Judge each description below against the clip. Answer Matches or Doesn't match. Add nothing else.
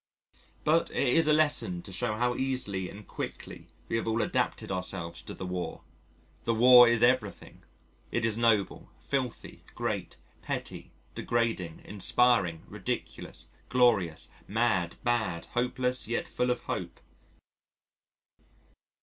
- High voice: Doesn't match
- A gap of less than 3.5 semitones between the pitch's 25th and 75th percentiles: Doesn't match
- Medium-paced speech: Doesn't match